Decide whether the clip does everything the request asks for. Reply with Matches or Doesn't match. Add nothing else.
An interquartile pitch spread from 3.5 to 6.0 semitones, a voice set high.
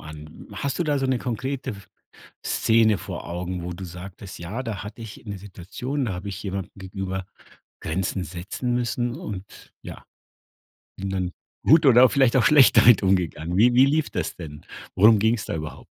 Doesn't match